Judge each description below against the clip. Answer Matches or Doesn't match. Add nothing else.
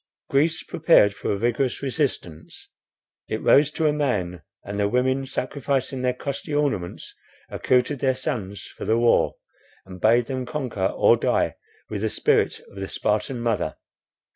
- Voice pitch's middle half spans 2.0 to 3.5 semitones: Doesn't match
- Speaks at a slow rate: Doesn't match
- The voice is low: Matches